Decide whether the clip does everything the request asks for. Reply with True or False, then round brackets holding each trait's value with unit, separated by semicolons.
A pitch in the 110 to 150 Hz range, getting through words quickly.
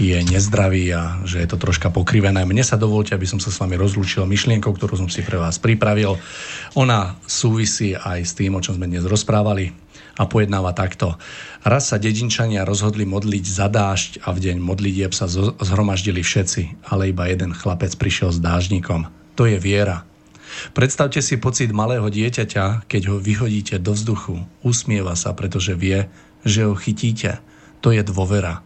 False (100 Hz; 170 wpm)